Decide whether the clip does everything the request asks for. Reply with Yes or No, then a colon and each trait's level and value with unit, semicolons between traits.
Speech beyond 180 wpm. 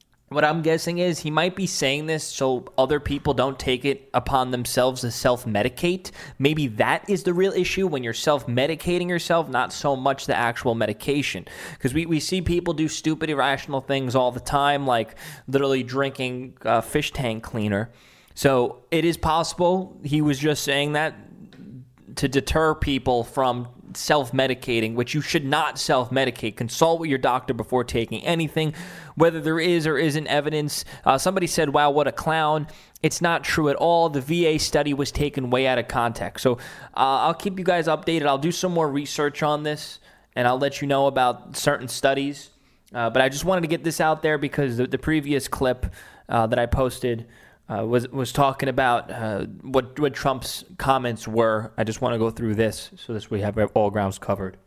Yes: average, 195 wpm